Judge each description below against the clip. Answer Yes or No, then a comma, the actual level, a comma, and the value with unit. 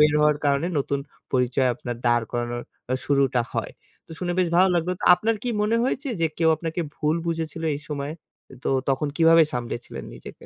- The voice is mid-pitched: Yes, medium, 150 Hz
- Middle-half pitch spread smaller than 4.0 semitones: No, average, 4.4 semitones